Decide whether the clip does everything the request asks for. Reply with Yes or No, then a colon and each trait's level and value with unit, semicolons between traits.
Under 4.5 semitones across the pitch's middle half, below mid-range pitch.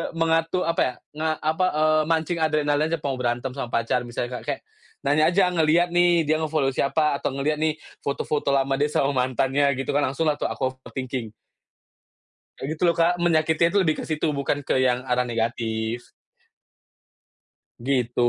No: average, 3.7 semitones; medium, 145 Hz